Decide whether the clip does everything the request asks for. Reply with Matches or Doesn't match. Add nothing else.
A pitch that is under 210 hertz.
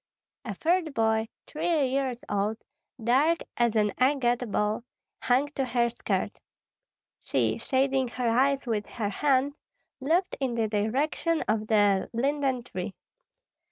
Doesn't match